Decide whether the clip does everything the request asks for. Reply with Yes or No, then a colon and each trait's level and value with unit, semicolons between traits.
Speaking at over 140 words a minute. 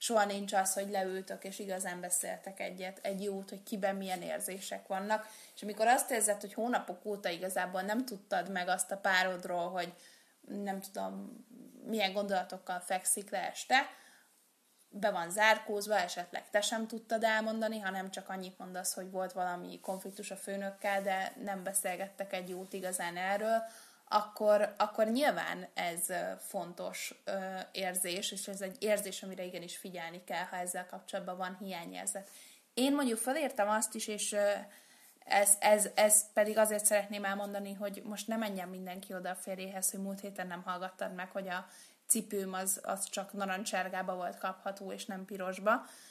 Yes: fast, 155 wpm